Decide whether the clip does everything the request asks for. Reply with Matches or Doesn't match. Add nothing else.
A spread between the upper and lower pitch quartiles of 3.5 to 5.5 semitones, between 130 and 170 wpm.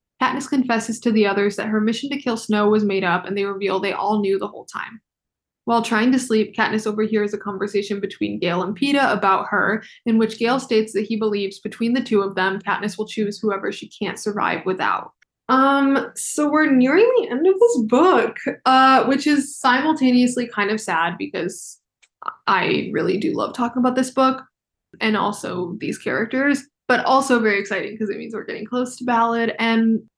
Doesn't match